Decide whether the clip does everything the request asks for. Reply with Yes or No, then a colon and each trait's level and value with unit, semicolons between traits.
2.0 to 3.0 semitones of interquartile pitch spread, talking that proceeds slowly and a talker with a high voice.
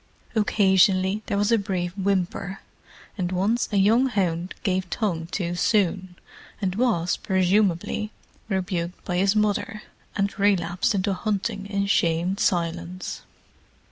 Yes: narrow, 2.5 semitones; slow, 125 wpm; high, 195 Hz